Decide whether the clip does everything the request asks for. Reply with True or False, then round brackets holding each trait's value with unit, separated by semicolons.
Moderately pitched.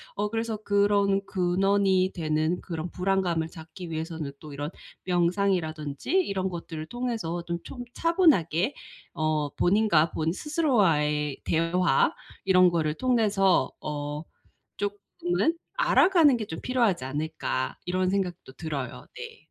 True (180 Hz)